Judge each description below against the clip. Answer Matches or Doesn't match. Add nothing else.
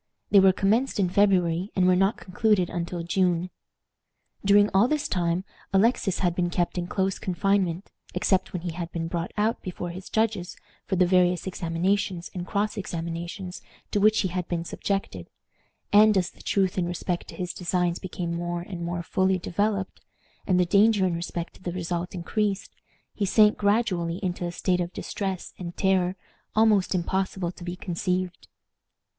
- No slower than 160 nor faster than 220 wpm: Matches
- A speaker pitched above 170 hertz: Matches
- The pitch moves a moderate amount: Doesn't match